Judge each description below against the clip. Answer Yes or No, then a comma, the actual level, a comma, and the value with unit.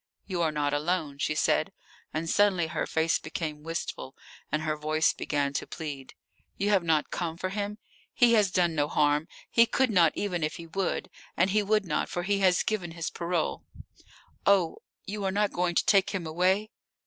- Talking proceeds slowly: No, average, 195 wpm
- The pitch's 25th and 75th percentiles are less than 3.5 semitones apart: No, average, 4.1 semitones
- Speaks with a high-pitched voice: No, medium, 175 Hz